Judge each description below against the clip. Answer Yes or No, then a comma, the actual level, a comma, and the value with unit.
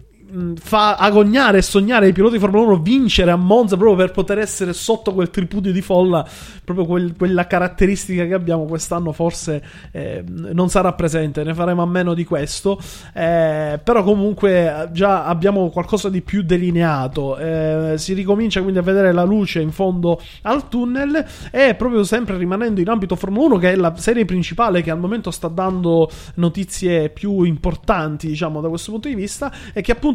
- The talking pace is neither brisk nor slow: No, fast, 180 wpm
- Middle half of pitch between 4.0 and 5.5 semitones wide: No, average, 3.3 semitones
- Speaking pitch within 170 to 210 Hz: Yes, medium, 185 Hz